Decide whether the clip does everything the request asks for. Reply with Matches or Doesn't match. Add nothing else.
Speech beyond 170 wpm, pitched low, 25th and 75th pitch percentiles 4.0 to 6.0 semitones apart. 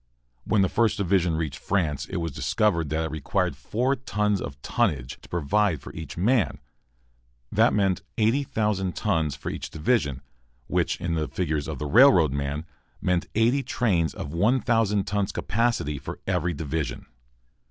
Doesn't match